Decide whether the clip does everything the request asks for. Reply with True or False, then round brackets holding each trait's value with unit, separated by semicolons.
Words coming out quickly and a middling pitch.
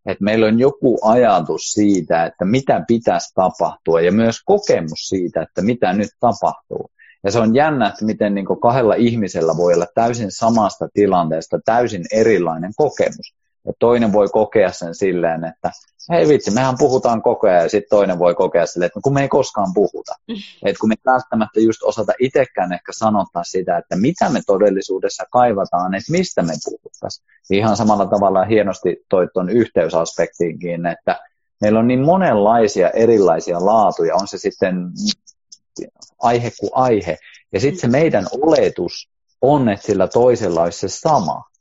False (160 wpm; 110 Hz)